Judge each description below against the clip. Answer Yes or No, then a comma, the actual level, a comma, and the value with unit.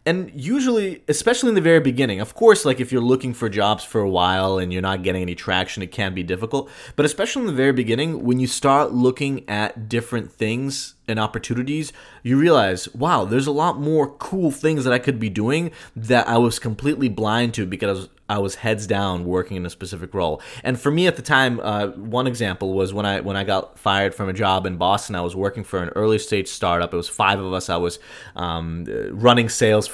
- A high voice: No, low, 115 Hz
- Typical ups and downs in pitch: No, wide, 5.8 semitones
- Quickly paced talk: Yes, fast, 225 wpm